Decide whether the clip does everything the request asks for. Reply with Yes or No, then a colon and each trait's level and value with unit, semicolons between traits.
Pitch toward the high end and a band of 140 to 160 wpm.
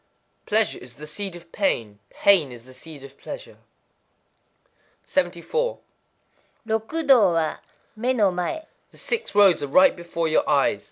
No: medium, 180 Hz; average, 145 wpm